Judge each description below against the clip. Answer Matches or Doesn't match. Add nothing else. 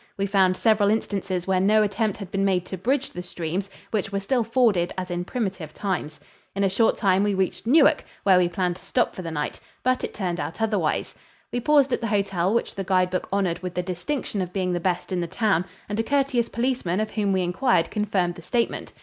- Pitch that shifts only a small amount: Doesn't match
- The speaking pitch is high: Matches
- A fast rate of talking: Matches